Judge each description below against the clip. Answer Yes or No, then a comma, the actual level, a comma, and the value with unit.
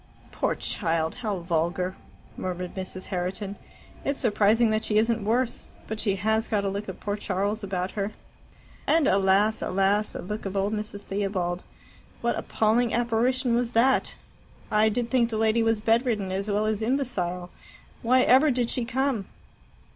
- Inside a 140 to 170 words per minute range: Yes, average, 160 wpm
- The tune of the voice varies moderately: Yes, average, 3.3 semitones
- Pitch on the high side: Yes, high, 215 Hz